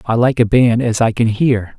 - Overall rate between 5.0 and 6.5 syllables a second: No, 4.8 syllables/s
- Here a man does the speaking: Yes, male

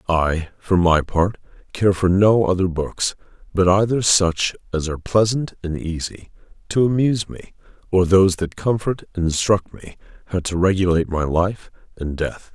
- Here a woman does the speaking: No, male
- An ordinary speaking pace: Yes, average, 165 wpm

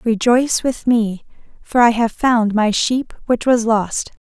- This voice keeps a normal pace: Yes, average, 170 wpm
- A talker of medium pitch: No, high, 230 Hz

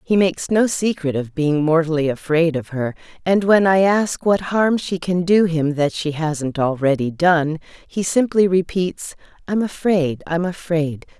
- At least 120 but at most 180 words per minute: Yes, average, 170 wpm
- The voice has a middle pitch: Yes, medium, 170 Hz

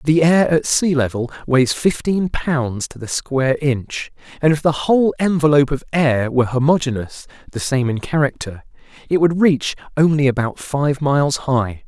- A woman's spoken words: No, male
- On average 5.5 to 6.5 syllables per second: No, 4.8 syllables/s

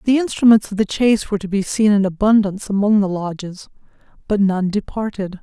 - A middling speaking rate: Yes, average, 190 wpm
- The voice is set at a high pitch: Yes, high, 205 Hz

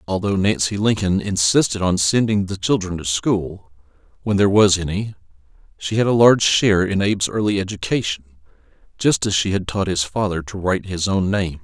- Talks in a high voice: No, very low, 95 Hz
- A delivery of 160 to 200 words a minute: Yes, average, 180 wpm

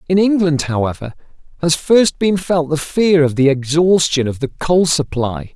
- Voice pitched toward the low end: No, medium, 160 Hz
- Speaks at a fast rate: No, average, 175 wpm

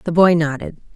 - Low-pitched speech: No, medium, 155 Hz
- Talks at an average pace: Yes, average, 190 wpm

